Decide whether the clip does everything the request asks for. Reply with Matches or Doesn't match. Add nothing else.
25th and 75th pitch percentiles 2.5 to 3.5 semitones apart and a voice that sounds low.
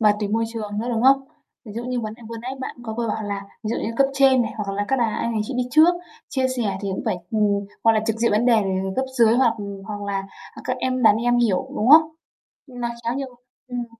Doesn't match